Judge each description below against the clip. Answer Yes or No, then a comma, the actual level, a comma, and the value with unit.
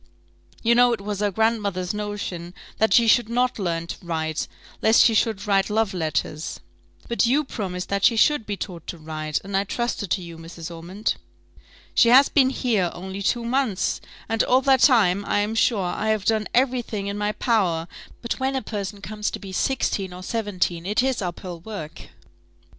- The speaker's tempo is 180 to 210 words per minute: Yes, average, 195 wpm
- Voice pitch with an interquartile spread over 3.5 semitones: Yes, average, 4.3 semitones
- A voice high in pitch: Yes, high, 205 Hz